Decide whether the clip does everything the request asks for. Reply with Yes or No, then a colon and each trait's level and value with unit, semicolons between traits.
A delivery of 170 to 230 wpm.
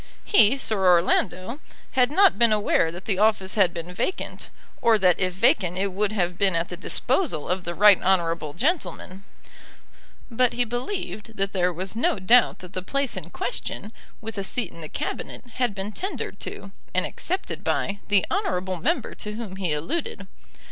Yes: average, 180 wpm